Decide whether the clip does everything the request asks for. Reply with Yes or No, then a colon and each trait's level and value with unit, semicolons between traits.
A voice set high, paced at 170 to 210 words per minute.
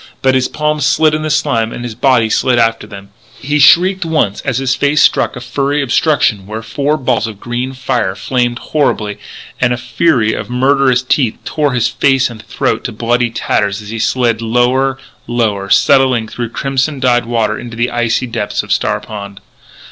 No: low, 125 Hz; average, 185 wpm